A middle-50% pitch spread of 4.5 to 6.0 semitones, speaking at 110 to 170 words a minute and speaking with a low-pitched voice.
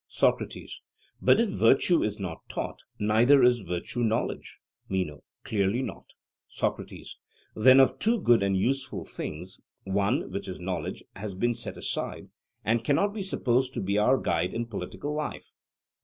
Yes: average, 5.2 semitones; average, 155 wpm; low, 115 Hz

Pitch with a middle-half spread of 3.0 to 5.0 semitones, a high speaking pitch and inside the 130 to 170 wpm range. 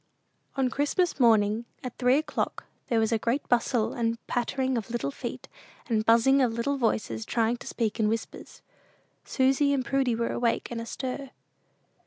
No: narrow, 2.6 semitones; high, 240 Hz; average, 165 wpm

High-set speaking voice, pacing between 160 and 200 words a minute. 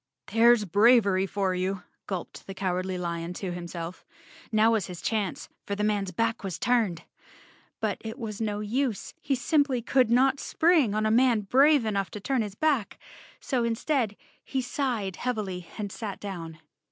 Yes: high, 215 Hz; average, 165 wpm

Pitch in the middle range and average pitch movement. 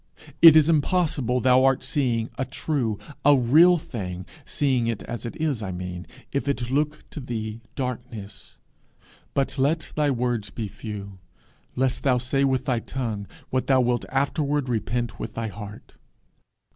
No: low, 125 Hz; average, 3.7 semitones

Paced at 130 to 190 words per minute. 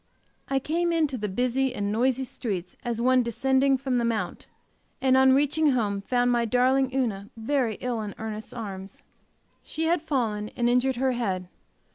Yes: average, 170 wpm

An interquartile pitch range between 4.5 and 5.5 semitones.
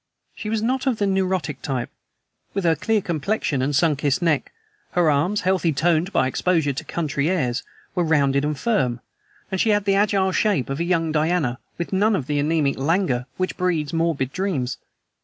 Yes: average, 5.1 semitones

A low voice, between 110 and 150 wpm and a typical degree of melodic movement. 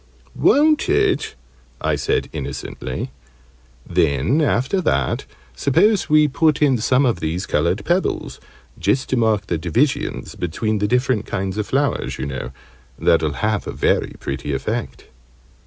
No: low, 110 Hz; average, 140 wpm; wide, 8.9 semitones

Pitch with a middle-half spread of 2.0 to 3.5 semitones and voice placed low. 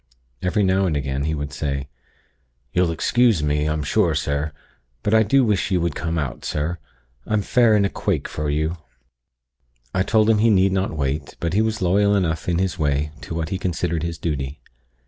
No: average, 4.7 semitones; very low, 85 Hz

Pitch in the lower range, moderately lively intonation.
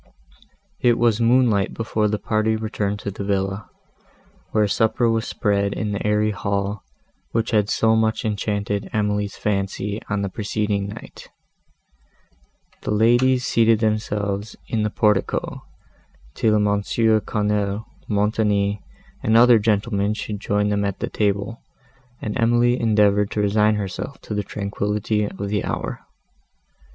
No: low, 105 Hz; narrow, 1.6 semitones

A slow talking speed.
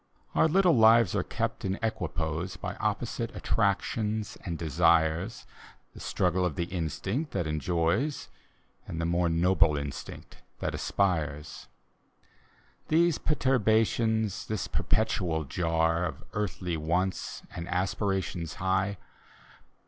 Yes: slow, 110 wpm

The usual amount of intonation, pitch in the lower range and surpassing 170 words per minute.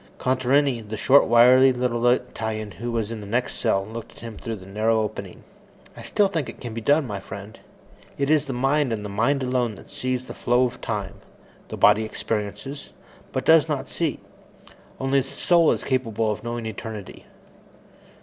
Yes: average, 3.4 semitones; low, 120 Hz; average, 190 wpm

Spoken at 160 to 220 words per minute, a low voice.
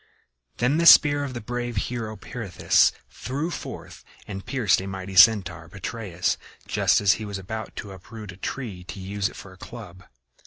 Yes: average, 180 wpm; low, 105 Hz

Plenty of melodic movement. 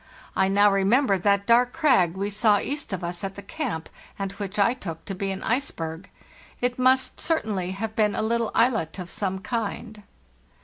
No: average, 3.5 semitones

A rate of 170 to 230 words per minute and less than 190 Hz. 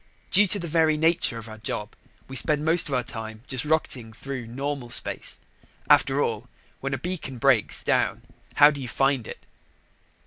Yes: average, 180 wpm; low, 135 Hz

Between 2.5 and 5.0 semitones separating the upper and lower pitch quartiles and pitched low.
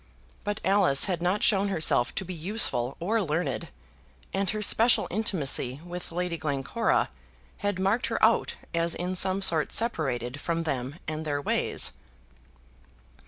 No: average, 4.5 semitones; medium, 175 Hz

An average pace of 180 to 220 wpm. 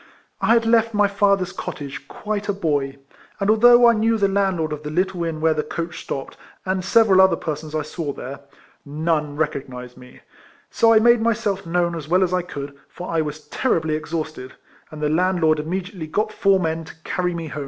Yes: average, 200 wpm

